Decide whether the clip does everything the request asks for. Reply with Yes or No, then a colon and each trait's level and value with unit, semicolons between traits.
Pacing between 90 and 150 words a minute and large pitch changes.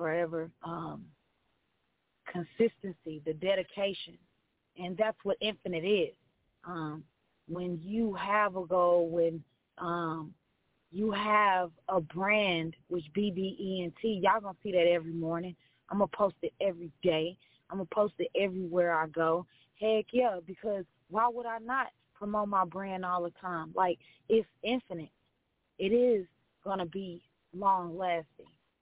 No: average, 140 wpm; average, 3.4 semitones